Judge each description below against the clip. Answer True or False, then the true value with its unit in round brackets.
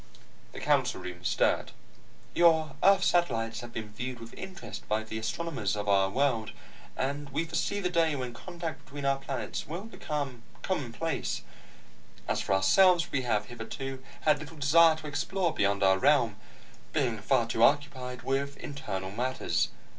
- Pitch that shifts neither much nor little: False (5.8 semitones)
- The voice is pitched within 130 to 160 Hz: True (135 Hz)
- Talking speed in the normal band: True (155 wpm)